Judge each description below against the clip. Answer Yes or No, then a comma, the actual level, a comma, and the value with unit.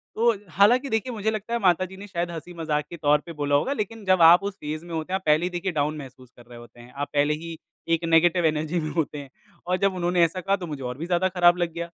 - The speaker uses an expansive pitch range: No, average, 3.8 semitones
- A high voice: No, medium, 170 Hz